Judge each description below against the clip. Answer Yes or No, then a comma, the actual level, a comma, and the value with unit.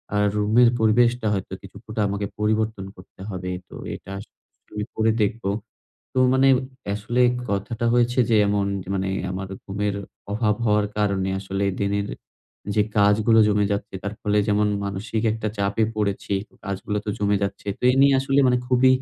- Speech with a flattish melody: Yes, narrow, 1.9 semitones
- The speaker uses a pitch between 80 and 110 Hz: Yes, low, 105 Hz